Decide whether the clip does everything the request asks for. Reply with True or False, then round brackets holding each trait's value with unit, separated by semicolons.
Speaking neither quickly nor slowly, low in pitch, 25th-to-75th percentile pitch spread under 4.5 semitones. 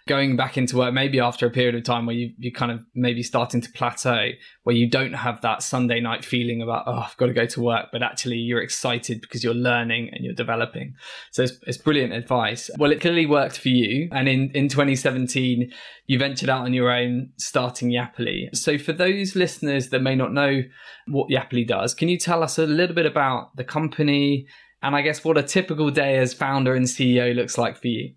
False (220 wpm; 125 Hz; 2.7 semitones)